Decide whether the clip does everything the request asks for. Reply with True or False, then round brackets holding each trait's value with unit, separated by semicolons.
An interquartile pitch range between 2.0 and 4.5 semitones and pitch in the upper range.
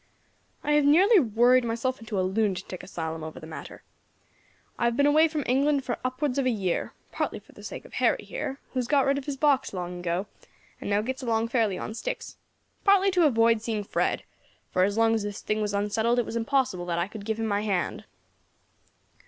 False (5.2 semitones; 230 Hz)